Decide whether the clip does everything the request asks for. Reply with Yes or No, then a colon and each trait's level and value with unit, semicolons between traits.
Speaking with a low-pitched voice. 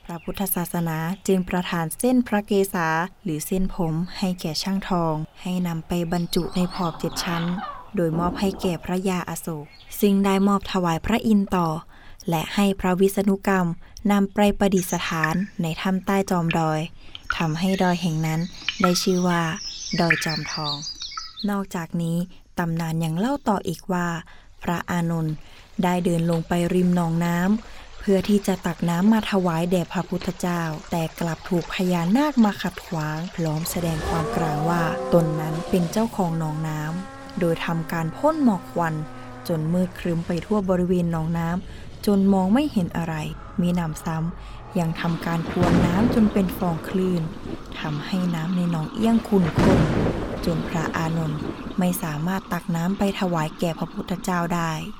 No: medium, 180 Hz